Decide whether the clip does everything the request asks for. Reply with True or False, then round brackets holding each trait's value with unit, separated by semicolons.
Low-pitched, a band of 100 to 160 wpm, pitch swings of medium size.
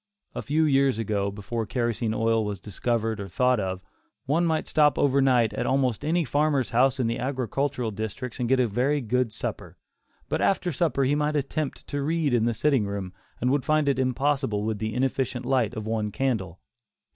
False (125 Hz; 195 wpm; 4.2 semitones)